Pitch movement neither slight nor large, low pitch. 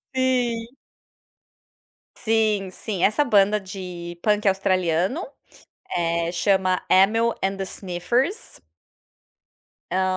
No: average, 3.4 semitones; high, 195 Hz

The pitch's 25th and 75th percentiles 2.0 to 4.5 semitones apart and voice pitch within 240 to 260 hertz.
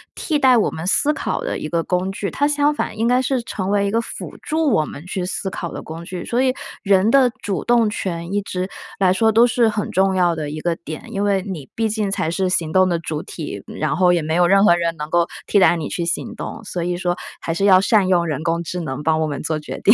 No: average, 4.1 semitones; medium, 185 Hz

